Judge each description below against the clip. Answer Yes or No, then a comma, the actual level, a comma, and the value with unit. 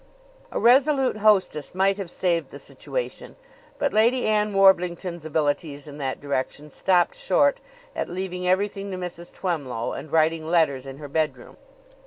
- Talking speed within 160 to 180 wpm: No, average, 150 wpm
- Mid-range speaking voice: Yes, medium, 180 Hz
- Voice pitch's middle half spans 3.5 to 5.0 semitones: Yes, average, 4.5 semitones